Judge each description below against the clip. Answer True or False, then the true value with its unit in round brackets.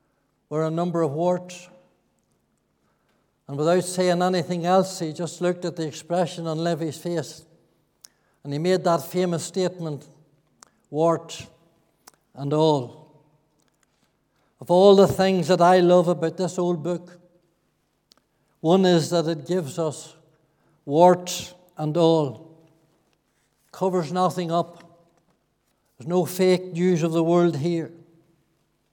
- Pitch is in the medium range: True (170 Hz)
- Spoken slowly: True (125 wpm)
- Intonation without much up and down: True (2.1 semitones)